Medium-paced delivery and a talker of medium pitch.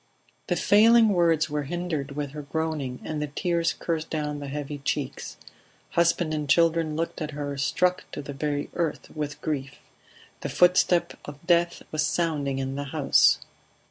Yes: average, 160 wpm; medium, 155 Hz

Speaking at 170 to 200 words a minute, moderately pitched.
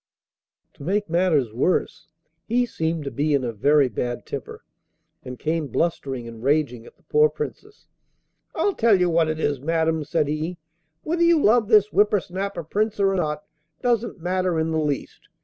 Yes: average, 175 wpm; medium, 160 Hz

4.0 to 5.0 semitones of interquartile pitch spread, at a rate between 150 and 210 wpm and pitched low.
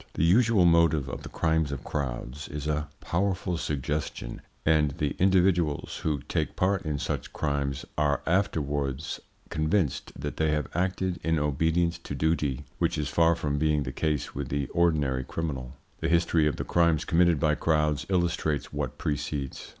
No: average, 2.7 semitones; average, 165 wpm; very low, 75 Hz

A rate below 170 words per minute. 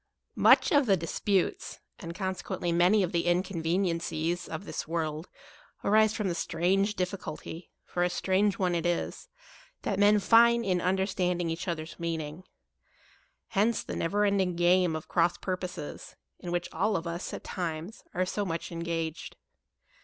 Yes: average, 155 wpm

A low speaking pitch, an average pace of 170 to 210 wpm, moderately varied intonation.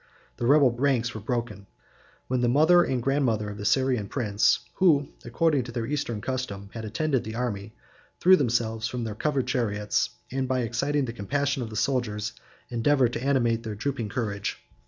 Yes: low, 120 Hz; average, 175 wpm; average, 3.7 semitones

